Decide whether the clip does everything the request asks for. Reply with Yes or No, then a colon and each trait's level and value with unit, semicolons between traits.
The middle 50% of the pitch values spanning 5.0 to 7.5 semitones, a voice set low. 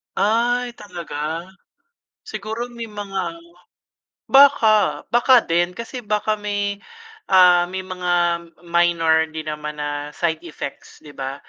No: average, 5.3 semitones; medium, 185 Hz